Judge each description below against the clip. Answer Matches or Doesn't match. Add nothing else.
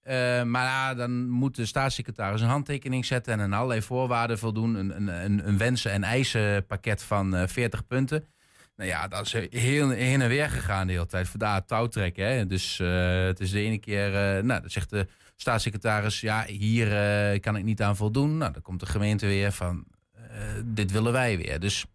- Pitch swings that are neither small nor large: Matches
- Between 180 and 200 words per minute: Matches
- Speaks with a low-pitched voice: Matches